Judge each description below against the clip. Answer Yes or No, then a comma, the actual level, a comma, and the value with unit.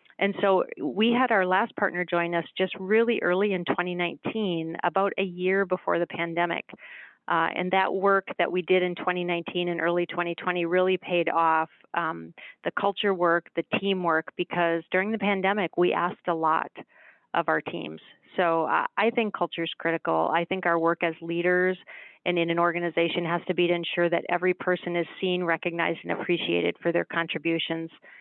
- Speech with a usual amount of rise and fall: No, narrow, 1.9 semitones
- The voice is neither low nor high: Yes, medium, 175 Hz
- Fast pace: No, average, 180 wpm